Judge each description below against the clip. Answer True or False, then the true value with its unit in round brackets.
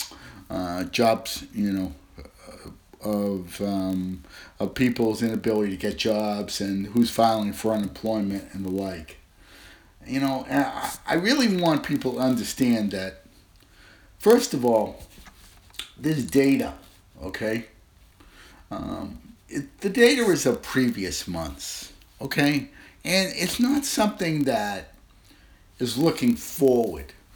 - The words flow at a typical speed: False (120 wpm)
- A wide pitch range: True (6.4 semitones)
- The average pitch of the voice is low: True (110 Hz)